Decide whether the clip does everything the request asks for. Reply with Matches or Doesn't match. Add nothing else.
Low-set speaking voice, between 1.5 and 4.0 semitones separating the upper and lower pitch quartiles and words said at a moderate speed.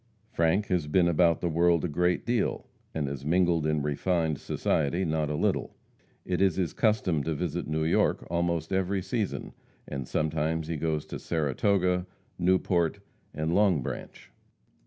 Matches